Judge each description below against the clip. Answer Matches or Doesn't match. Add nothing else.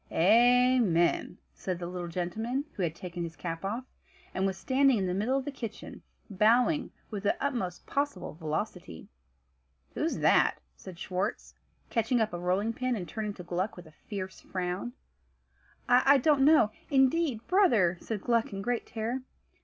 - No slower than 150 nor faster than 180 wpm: Matches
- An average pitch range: Doesn't match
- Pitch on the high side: Matches